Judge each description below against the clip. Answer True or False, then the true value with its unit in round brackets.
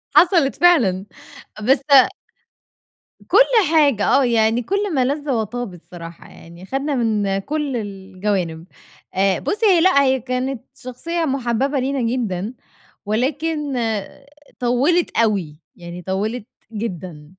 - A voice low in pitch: False (245 Hz)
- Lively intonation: True (6.3 semitones)